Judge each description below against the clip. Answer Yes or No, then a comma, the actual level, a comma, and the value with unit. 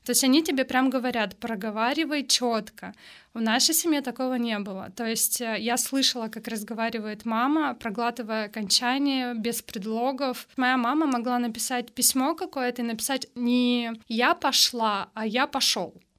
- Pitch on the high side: Yes, high, 245 Hz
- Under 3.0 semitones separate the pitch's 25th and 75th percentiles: Yes, narrow, 2.5 semitones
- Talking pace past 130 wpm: Yes, average, 145 wpm